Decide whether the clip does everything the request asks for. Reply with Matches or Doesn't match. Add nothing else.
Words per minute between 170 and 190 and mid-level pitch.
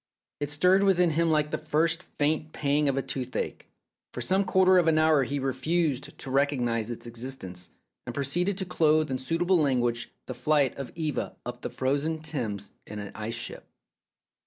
Matches